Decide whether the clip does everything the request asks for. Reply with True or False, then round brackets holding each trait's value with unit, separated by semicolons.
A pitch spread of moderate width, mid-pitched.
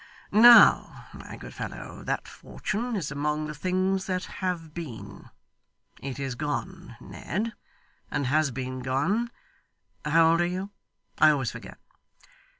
True (4.8 semitones; 165 Hz)